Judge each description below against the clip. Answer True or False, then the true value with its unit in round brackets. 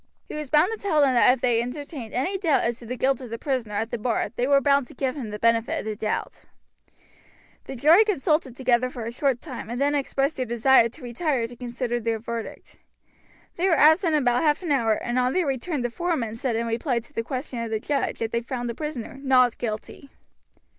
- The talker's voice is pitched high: True (255 Hz)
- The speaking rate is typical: False (235 wpm)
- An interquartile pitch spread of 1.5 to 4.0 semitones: True (3.6 semitones)